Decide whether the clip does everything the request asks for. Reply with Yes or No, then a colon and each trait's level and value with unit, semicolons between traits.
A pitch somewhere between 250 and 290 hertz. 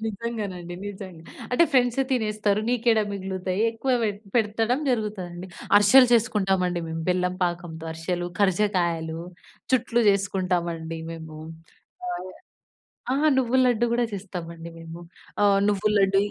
No: high, 195 Hz